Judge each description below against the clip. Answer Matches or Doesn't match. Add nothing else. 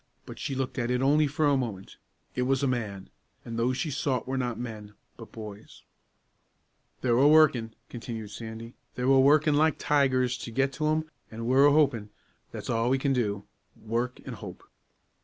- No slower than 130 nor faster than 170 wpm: Doesn't match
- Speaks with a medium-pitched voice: Doesn't match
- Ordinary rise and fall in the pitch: Matches